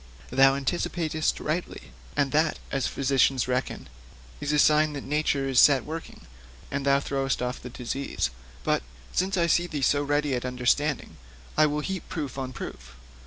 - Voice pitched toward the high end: No, medium, 140 Hz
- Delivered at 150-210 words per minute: Yes, average, 165 wpm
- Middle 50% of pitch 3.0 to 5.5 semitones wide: No, narrow, 2.5 semitones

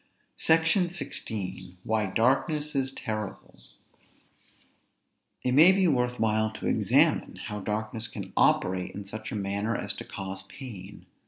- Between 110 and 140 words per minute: Yes, slow, 135 wpm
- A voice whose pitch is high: No, low, 110 Hz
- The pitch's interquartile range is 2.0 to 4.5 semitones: No, average, 5.2 semitones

